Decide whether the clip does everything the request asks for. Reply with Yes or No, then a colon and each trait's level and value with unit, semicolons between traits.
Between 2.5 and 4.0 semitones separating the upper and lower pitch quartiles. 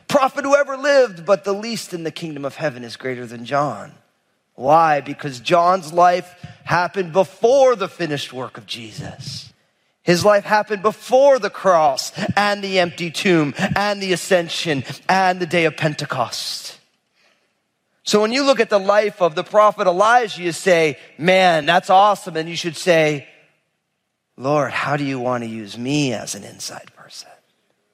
No: wide, 5.6 semitones